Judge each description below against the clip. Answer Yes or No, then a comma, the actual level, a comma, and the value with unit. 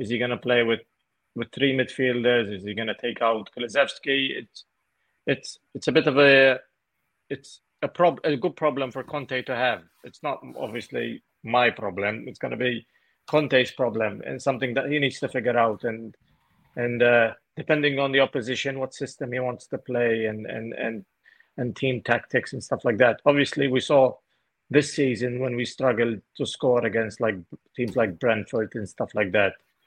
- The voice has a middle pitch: No, low, 125 Hz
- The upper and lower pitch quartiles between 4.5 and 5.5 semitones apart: No, average, 2.7 semitones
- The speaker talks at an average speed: Yes, average, 185 wpm